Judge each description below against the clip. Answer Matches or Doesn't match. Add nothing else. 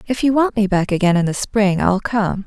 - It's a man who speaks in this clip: Doesn't match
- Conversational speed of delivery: Doesn't match